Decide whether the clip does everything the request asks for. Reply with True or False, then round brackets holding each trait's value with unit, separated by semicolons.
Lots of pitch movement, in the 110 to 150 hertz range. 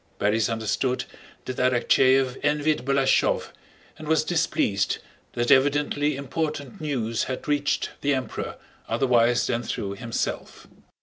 False (3.5 semitones; 135 Hz)